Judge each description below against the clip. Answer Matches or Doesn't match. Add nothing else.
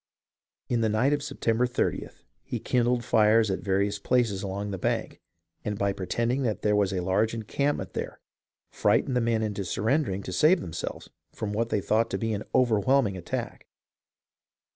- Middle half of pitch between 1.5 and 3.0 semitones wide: Doesn't match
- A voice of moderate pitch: Doesn't match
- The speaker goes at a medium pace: Matches